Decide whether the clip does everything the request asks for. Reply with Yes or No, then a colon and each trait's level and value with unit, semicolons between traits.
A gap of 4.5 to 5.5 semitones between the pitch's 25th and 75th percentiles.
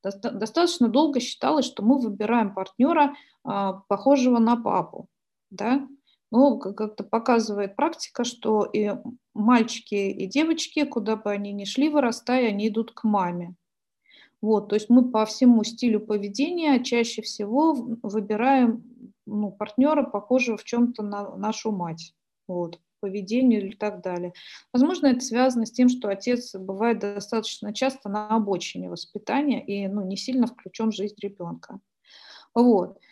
No: average, 3.6 semitones